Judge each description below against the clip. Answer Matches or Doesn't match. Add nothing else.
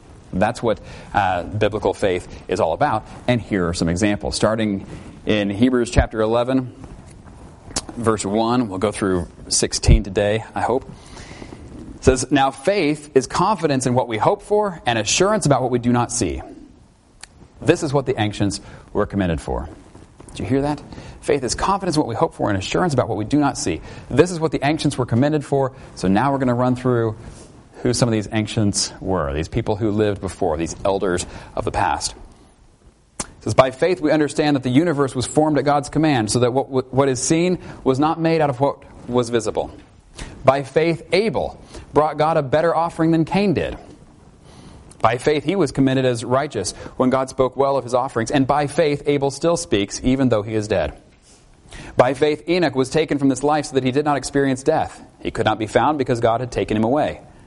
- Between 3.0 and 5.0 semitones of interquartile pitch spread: Doesn't match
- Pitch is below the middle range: Matches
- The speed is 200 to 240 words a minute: Matches